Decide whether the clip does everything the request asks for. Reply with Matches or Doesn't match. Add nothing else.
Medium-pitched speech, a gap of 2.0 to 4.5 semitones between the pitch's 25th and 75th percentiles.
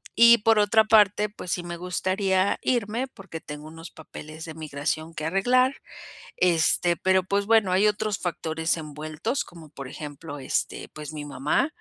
Doesn't match